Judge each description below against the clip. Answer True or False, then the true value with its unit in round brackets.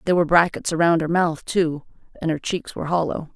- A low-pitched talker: False (165 Hz)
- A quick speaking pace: True (215 wpm)